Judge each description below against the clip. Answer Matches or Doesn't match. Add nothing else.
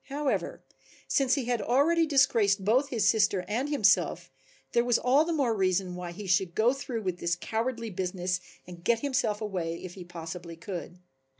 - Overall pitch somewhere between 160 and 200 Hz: Doesn't match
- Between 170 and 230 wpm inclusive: Matches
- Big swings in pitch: Matches